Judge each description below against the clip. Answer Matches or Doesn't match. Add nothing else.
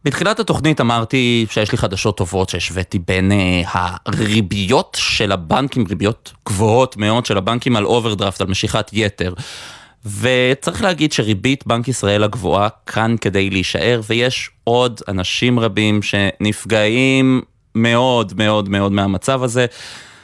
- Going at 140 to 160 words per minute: Doesn't match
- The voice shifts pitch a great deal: Doesn't match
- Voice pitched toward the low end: Matches